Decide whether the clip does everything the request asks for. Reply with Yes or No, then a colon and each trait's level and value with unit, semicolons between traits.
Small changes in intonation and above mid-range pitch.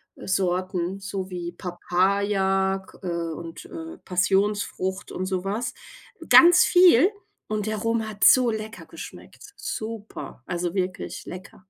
No: average, 3.0 semitones; high, 195 Hz